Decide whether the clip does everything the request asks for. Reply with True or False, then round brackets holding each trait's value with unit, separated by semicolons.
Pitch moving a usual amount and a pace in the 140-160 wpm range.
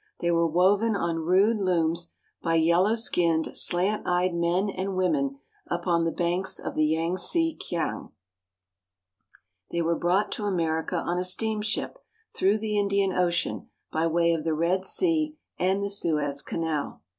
True (3.1 semitones; 150 wpm)